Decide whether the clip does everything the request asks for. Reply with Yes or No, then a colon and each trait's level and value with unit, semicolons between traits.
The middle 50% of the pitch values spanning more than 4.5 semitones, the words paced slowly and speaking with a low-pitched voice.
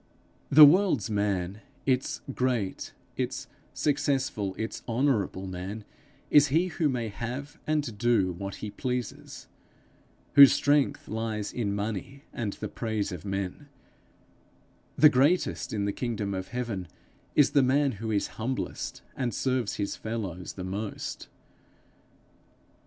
Yes: average, 5.2 semitones; slow, 130 wpm; low, 115 Hz